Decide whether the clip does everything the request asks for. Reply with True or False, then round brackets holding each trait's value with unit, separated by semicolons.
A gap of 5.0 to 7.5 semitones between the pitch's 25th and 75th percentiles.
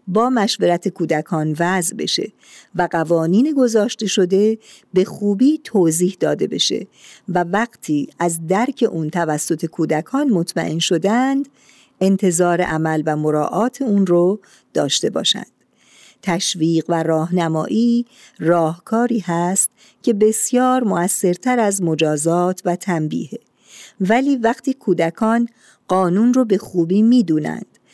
True (5.3 semitones)